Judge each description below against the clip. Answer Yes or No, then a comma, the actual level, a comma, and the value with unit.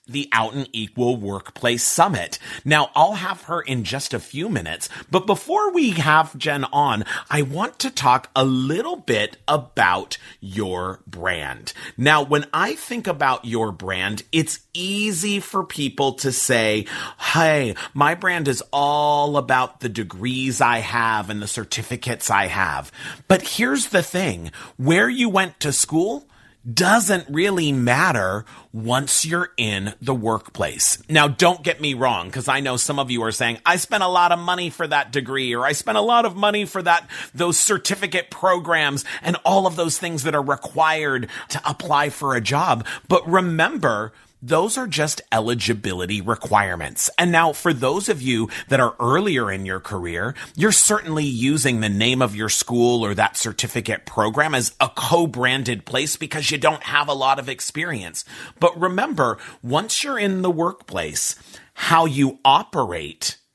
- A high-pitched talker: No, medium, 140 Hz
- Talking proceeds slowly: No, average, 165 wpm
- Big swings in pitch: Yes, wide, 6.3 semitones